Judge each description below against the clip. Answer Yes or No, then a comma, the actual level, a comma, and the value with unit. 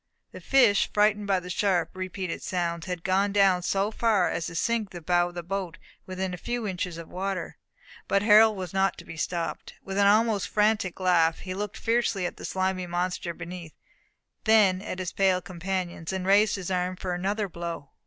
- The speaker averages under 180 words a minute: No, average, 200 wpm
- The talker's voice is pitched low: No, medium, 185 Hz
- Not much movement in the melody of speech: Yes, narrow, 2.3 semitones